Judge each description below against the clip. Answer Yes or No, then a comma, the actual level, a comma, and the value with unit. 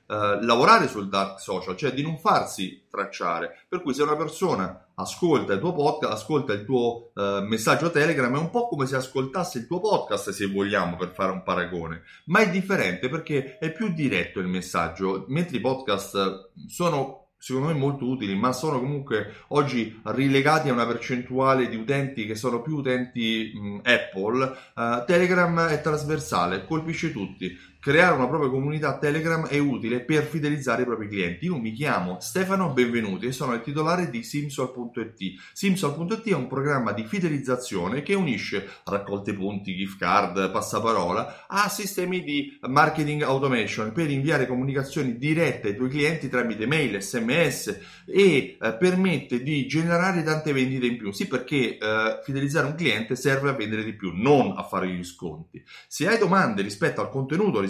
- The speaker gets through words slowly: No, average, 165 wpm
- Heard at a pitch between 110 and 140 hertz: Yes, low, 135 Hz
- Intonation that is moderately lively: No, wide, 6.1 semitones